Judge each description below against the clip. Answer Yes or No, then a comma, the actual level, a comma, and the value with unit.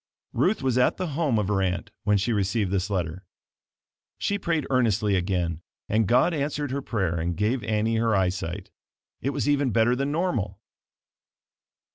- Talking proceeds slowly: No, average, 165 wpm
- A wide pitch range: Yes, wide, 6.0 semitones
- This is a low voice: Yes, low, 110 Hz